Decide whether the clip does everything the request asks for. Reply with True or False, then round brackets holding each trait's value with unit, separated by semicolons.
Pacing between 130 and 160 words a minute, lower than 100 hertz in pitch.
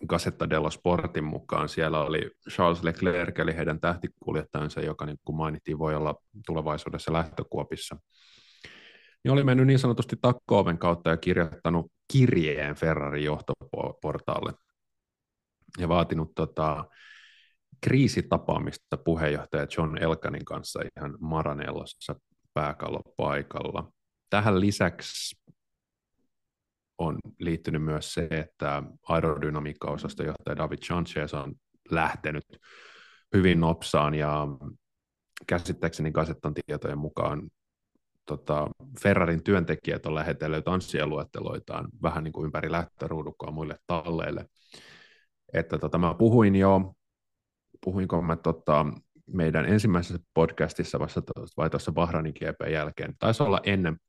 False (105 wpm; 80 Hz)